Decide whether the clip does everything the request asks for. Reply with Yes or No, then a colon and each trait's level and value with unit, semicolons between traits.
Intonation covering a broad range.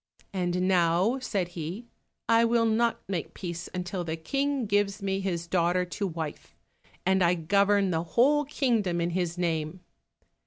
No: average, 3.6 semitones